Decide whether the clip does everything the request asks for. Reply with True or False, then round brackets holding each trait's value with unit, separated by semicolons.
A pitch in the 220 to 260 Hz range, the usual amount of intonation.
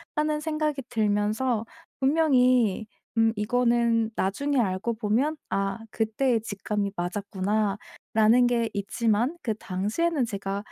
True (225 Hz; 3.6 semitones)